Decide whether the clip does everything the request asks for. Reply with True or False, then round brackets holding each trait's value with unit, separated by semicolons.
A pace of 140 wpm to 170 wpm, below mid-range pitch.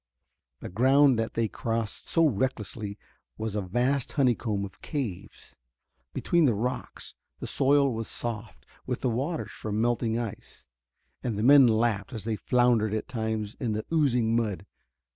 True (155 wpm; 115 Hz)